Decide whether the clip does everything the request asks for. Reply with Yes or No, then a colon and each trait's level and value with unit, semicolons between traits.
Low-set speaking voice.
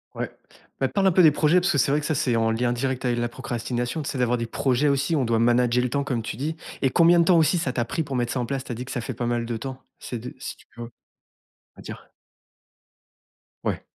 Yes: low, 125 Hz